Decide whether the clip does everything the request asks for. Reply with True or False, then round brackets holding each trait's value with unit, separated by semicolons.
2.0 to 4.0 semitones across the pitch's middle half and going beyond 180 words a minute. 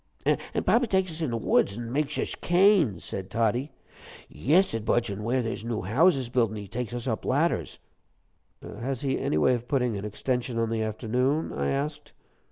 False (4.4 semitones; 190 wpm)